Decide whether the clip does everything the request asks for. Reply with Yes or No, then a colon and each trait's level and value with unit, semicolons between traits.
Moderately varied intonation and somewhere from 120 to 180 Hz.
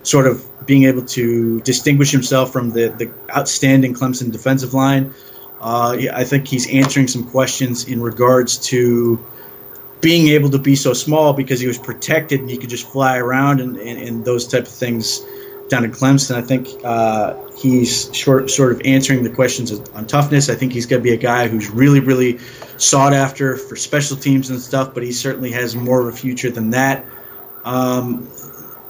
No: narrow, 1.7 semitones; low, 130 Hz